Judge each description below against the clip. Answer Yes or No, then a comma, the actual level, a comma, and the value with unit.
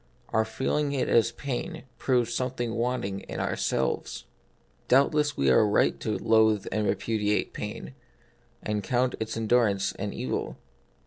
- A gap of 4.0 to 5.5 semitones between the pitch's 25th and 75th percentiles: No, average, 3.3 semitones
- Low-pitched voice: Yes, low, 115 Hz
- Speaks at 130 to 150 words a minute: Yes, average, 145 wpm